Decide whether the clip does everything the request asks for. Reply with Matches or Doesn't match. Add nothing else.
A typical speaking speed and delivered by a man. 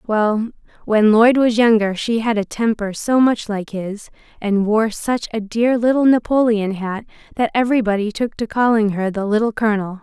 Doesn't match